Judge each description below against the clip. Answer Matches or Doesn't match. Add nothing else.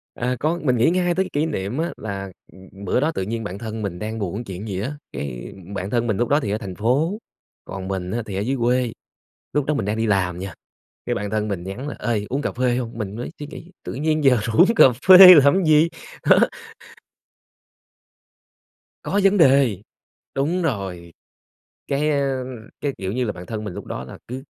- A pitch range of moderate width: Doesn't match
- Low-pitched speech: Matches